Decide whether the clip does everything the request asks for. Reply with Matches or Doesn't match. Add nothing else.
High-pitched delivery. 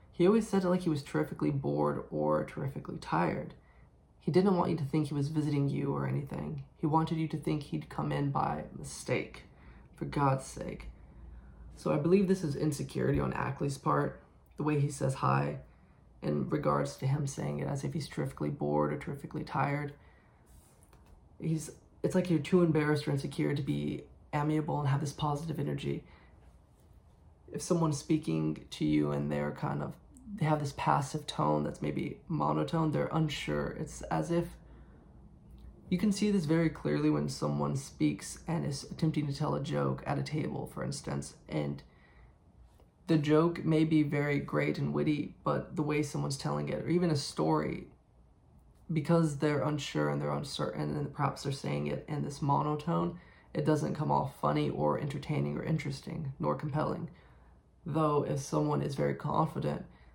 Doesn't match